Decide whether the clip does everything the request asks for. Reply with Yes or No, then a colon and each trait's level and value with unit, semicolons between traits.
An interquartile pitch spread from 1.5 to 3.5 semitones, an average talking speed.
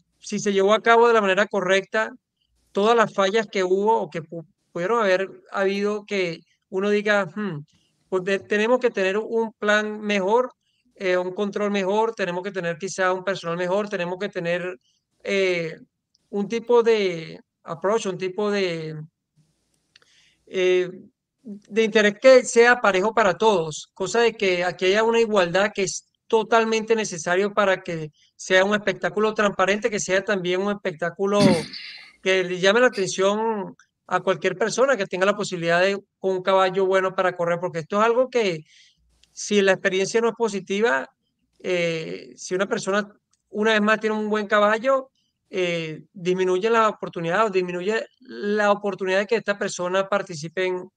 Yes: average, 2.7 semitones; average, 160 wpm